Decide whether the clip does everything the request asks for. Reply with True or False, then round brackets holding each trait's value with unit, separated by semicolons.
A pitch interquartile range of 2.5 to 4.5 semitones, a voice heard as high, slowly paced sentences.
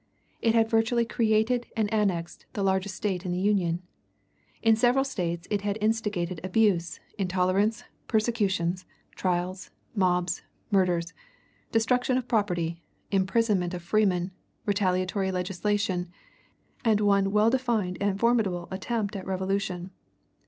True (3.3 semitones; 195 Hz; 120 wpm)